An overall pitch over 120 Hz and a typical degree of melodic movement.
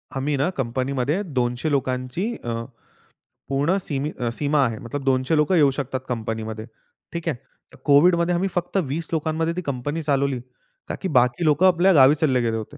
Yes: medium, 140 Hz; average, 4.3 semitones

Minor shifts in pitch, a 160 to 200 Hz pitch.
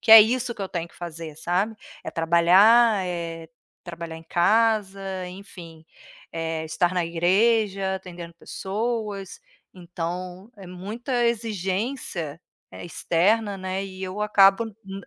No: average, 3.7 semitones; high, 190 Hz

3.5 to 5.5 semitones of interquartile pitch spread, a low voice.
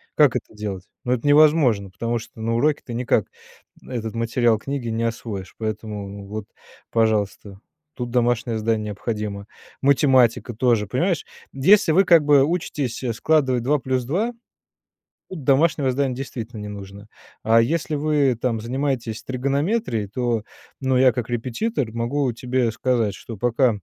Yes: average, 3.8 semitones; low, 120 Hz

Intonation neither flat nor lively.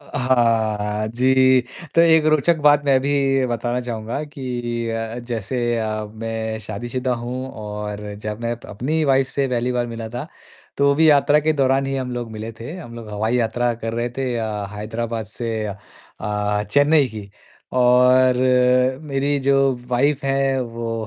Yes: average, 3.4 semitones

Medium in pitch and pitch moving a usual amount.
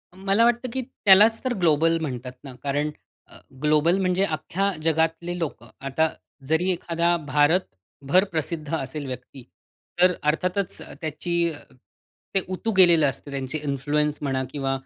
Yes: medium, 160 Hz; average, 4.1 semitones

